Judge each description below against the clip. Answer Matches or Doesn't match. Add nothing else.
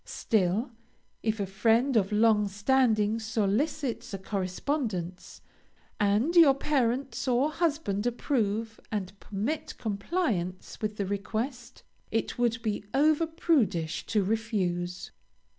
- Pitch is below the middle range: Doesn't match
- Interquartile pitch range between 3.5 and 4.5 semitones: Doesn't match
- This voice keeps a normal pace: Doesn't match